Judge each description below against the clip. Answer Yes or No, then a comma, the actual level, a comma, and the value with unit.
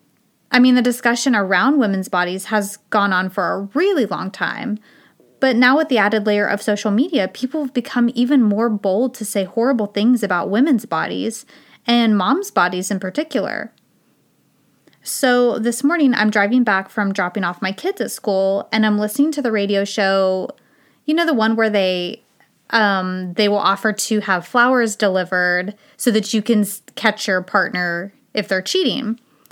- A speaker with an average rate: Yes, average, 175 wpm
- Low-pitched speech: No, high, 215 Hz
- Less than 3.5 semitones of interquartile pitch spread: No, average, 4.0 semitones